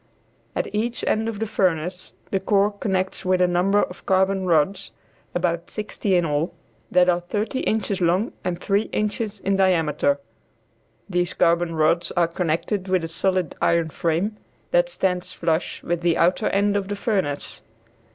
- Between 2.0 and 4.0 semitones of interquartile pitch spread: Yes, average, 2.9 semitones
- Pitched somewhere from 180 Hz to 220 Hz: Yes, medium, 185 Hz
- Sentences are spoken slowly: No, average, 160 wpm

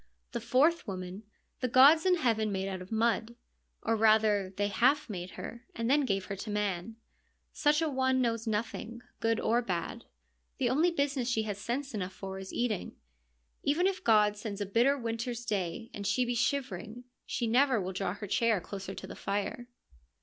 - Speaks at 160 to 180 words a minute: No, average, 195 wpm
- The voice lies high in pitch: Yes, high, 225 Hz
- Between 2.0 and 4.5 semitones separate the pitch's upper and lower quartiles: Yes, average, 4.0 semitones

